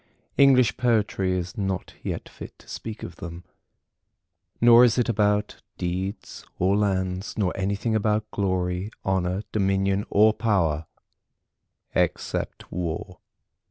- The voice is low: Yes, low, 100 Hz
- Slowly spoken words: Yes, slow, 120 wpm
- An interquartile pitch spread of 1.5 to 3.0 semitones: Yes, average, 2.7 semitones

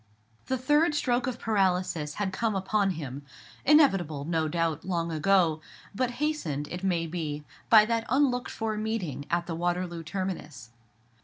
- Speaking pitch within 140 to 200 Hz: Yes, medium, 185 Hz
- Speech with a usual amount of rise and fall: No, wide, 5.7 semitones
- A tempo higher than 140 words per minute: Yes, average, 150 wpm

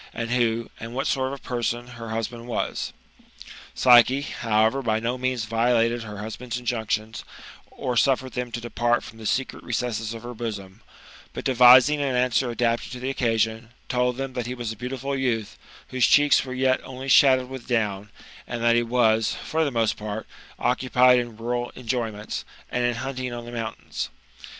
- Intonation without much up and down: Yes, narrow, 1.9 semitones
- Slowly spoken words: No, average, 185 wpm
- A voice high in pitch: No, low, 120 Hz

